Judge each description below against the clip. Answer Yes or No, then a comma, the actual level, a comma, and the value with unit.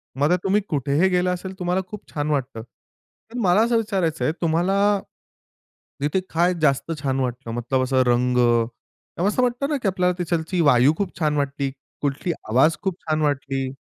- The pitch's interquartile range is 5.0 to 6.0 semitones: Yes, average, 5.3 semitones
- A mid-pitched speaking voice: Yes, medium, 155 Hz